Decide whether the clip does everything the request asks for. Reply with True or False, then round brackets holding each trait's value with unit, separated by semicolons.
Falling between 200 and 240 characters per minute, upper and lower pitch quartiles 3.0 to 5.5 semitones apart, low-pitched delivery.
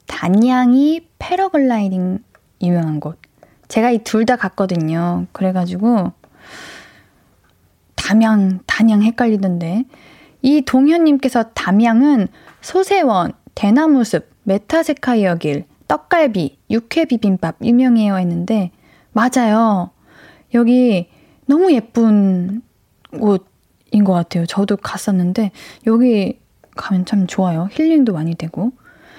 False (225 characters per minute; 5.2 semitones; 215 Hz)